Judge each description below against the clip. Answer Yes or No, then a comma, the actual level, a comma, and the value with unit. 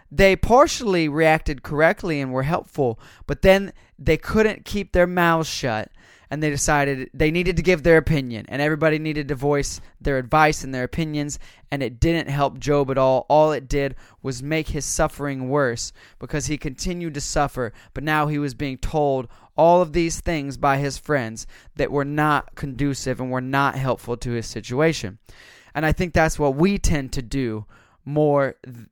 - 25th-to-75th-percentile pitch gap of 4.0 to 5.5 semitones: No, average, 3.5 semitones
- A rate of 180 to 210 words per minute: Yes, average, 185 wpm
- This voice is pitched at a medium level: Yes, medium, 145 Hz